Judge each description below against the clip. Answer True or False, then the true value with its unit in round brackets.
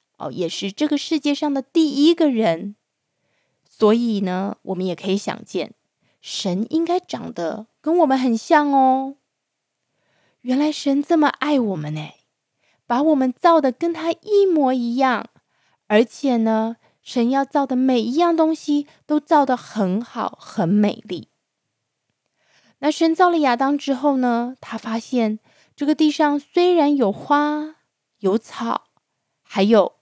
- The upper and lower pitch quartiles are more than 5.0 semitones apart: True (5.5 semitones)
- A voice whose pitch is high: True (265 Hz)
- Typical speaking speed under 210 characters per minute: True (195 characters per minute)